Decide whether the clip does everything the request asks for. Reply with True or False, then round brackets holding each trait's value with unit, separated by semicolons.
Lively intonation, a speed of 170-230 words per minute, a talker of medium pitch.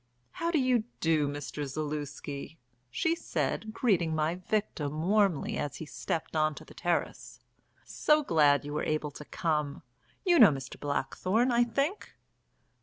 False (6.9 semitones; 150 wpm; 160 Hz)